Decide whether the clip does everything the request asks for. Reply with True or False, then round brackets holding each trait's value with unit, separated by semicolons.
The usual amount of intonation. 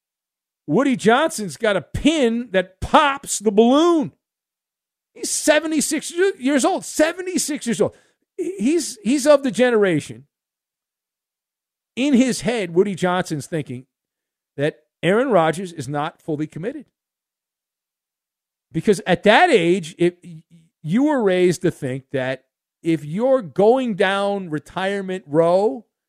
False (8.3 semitones)